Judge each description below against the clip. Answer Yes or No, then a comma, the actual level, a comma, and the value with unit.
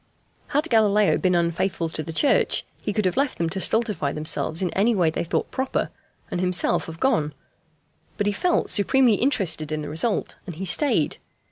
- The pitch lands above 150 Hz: Yes, high, 190 Hz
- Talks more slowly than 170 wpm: No, average, 190 wpm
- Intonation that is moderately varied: No, wide, 5.7 semitones